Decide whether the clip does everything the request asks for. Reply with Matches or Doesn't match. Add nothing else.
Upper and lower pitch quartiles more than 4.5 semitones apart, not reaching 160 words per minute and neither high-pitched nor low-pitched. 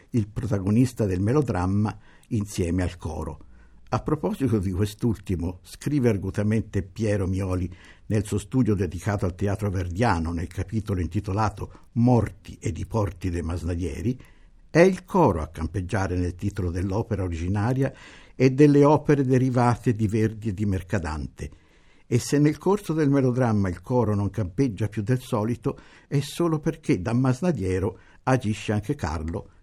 Doesn't match